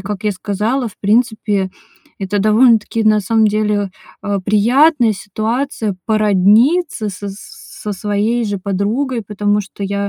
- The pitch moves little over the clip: Yes, narrow, 2.1 semitones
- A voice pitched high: Yes, high, 210 Hz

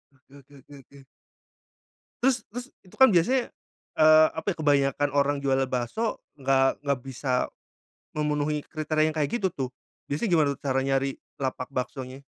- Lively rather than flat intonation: No, narrow, 2.6 semitones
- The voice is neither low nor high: Yes, medium, 145 Hz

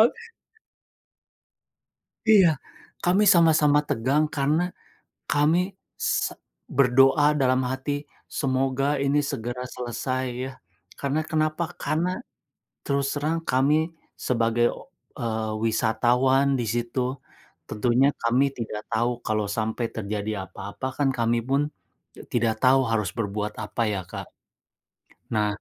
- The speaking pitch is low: Yes, low, 130 Hz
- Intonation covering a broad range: No, average, 4.2 semitones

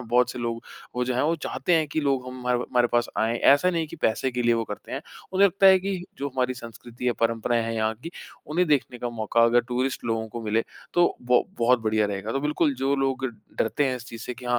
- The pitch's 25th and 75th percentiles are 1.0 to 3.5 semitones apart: Yes, average, 3.2 semitones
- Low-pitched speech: Yes, low, 125 Hz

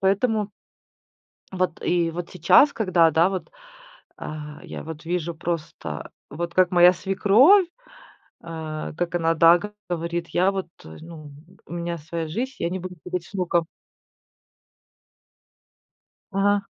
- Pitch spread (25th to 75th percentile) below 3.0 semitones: Yes, narrow, 2.5 semitones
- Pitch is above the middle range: No, medium, 175 Hz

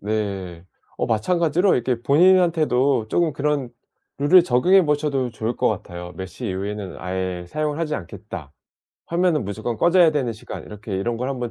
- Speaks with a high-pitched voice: No, low, 125 Hz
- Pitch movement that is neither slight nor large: No, wide, 7.0 semitones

